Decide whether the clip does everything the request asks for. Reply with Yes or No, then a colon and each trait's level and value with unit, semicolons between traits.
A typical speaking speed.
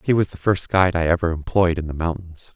No: fast, 260 wpm